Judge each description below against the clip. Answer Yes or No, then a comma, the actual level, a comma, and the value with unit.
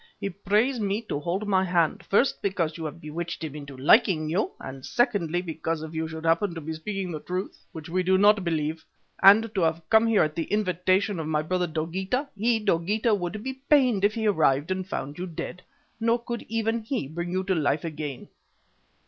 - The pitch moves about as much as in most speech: Yes, average, 4.7 semitones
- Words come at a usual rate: No, fast, 210 wpm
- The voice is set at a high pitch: No, medium, 180 Hz